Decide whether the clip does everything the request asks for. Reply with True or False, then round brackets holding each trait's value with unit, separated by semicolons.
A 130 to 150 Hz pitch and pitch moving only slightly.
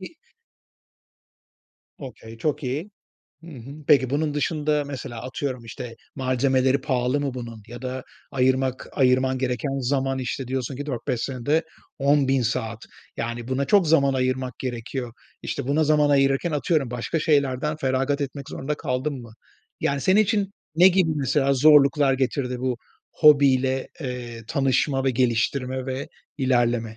True (135 Hz; 2.3 semitones)